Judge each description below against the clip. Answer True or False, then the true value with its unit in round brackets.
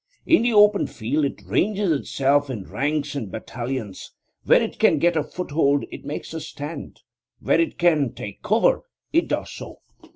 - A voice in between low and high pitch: True (150 Hz)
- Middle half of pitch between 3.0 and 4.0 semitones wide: False (5.0 semitones)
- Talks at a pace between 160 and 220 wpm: True (170 wpm)